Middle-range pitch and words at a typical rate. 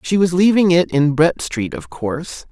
No: medium, 165 Hz; fast, 215 wpm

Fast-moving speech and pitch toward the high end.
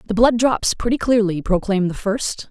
No: average, 190 wpm; high, 215 Hz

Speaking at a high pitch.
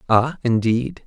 No: low, 120 Hz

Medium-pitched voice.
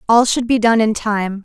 No: high, 220 Hz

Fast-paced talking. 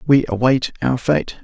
No: average, 165 wpm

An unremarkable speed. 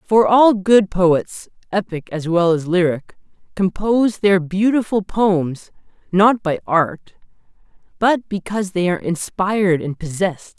No: slow, 130 wpm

